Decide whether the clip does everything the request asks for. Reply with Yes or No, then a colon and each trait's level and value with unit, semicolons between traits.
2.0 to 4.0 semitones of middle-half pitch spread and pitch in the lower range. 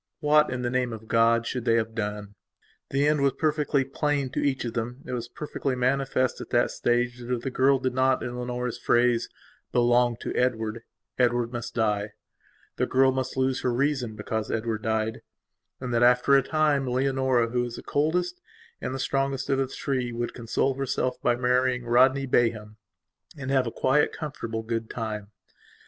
Yes: narrow, 2.4 semitones; low, 125 Hz